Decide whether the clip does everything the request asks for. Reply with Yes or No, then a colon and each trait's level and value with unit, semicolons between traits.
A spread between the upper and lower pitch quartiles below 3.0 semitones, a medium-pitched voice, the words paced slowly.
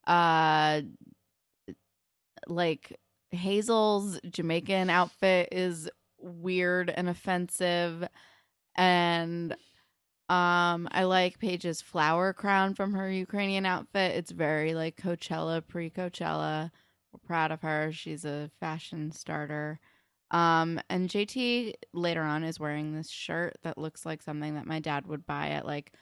Yes: narrow, 2.6 semitones; medium, 170 Hz; slow, 125 wpm